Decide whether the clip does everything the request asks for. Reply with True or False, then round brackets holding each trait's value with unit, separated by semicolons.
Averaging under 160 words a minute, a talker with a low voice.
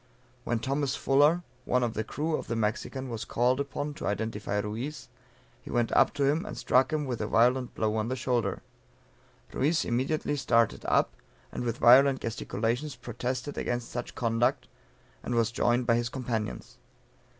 False (165 wpm; 125 Hz)